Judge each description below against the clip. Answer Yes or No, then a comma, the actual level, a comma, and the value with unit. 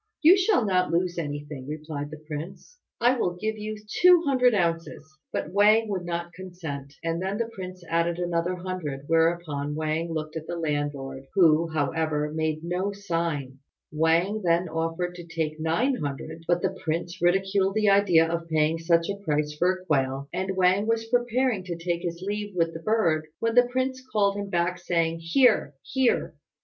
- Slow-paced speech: No, average, 180 wpm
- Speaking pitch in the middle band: Yes, medium, 170 Hz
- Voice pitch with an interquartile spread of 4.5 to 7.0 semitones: No, average, 4.0 semitones